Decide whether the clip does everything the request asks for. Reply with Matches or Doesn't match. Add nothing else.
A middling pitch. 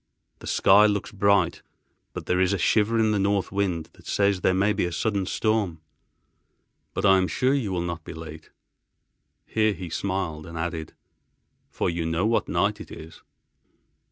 Doesn't match